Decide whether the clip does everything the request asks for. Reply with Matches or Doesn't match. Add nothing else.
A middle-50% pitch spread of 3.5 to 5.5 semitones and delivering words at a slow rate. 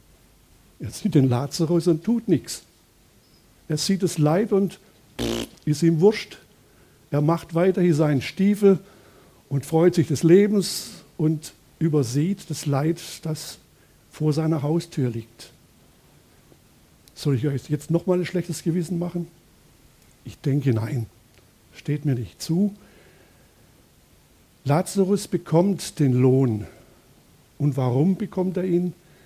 Matches